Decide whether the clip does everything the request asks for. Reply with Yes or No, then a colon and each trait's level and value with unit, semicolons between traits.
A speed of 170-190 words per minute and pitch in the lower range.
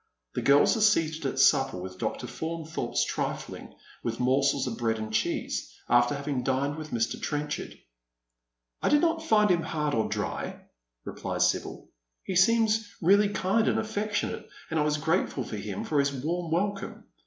No: average, 175 wpm; medium, 150 Hz